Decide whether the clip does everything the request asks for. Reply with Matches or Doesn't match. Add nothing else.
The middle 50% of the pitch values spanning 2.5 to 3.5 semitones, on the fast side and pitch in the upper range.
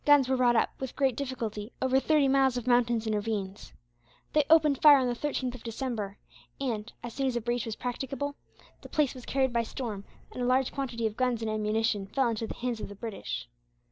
Matches